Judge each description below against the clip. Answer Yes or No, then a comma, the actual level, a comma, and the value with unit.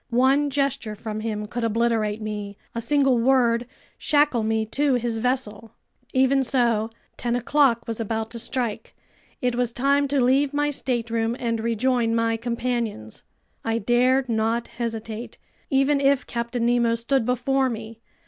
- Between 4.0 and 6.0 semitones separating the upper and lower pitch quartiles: No, narrow, 2.6 semitones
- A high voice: Yes, high, 235 Hz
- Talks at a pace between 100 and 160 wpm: Yes, average, 150 wpm